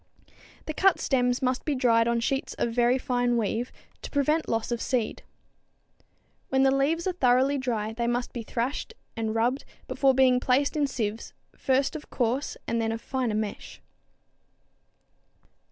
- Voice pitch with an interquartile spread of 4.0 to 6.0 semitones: No, average, 2.8 semitones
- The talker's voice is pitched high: Yes, very high, 250 Hz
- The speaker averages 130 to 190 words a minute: Yes, average, 160 wpm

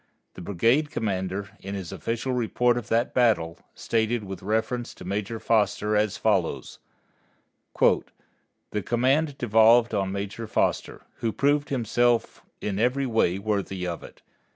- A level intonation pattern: No, average, 3.4 semitones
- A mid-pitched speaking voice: No, low, 110 Hz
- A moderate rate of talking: No, slow, 130 wpm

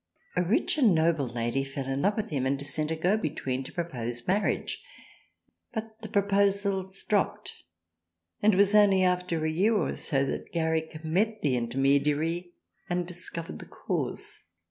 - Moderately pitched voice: Yes, medium, 170 Hz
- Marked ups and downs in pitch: Yes, wide, 6.1 semitones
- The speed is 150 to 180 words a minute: Yes, average, 170 wpm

